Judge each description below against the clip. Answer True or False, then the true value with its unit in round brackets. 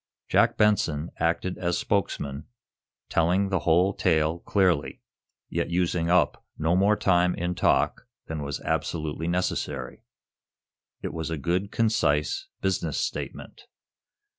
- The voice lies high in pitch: False (85 Hz)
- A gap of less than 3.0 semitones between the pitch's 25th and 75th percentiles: True (2.5 semitones)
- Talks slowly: True (120 wpm)